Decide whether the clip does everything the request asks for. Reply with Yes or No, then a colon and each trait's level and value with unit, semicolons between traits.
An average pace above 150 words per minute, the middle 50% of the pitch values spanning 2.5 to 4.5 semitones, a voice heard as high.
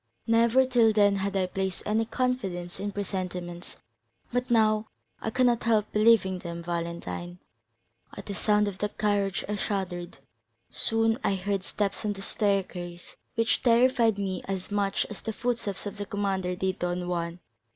Yes: average, 160 wpm; average, 3.3 semitones; high, 200 Hz